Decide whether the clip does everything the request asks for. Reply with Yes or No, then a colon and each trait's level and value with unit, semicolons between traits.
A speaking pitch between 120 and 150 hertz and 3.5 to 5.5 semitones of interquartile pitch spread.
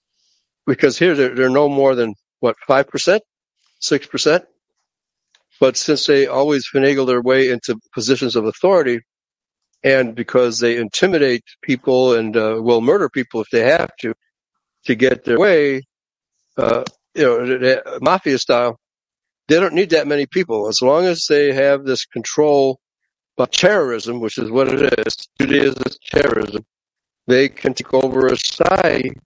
No: low, 130 Hz; narrow, 2.4 semitones